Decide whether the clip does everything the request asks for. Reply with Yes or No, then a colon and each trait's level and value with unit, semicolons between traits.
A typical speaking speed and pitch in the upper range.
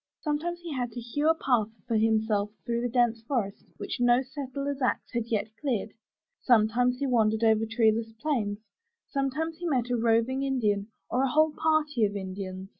Yes: average, 180 wpm; high, 240 Hz